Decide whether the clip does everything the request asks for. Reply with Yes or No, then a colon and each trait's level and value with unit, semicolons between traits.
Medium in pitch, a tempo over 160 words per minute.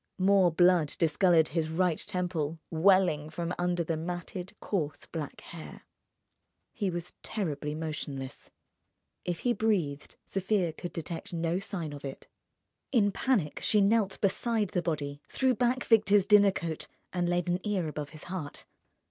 No: medium, 175 Hz; average, 150 wpm